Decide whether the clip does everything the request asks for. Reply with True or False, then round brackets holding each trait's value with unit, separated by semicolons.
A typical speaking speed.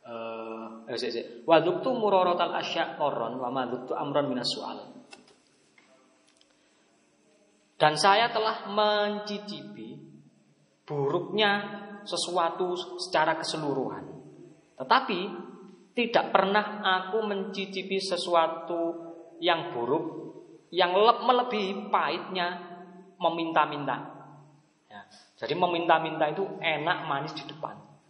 False (65 wpm)